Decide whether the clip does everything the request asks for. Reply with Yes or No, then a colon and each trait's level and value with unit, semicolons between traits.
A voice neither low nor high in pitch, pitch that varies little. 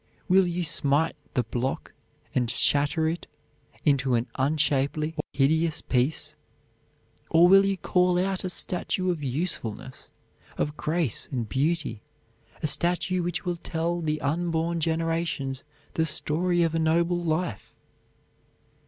No: medium, 160 Hz; average, 3.7 semitones